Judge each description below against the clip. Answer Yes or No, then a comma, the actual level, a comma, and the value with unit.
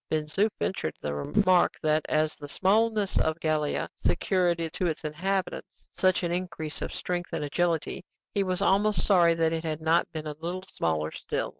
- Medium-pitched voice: Yes, medium, 170 Hz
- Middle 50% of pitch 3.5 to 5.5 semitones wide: No, average, 3.1 semitones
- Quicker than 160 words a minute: Yes, average, 180 wpm